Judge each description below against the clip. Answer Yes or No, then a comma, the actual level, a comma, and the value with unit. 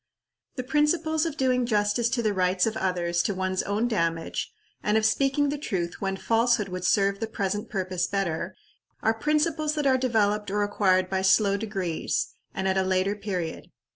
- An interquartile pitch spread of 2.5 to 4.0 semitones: No, average, 4.4 semitones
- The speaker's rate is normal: Yes, average, 180 wpm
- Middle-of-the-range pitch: No, high, 205 Hz